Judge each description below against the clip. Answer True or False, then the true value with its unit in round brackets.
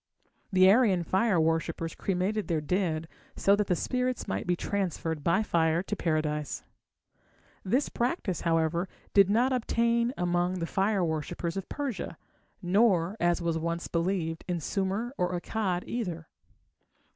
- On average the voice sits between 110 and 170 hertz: False (180 Hz)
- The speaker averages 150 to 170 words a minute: False (140 wpm)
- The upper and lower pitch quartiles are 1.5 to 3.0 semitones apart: False (3.7 semitones)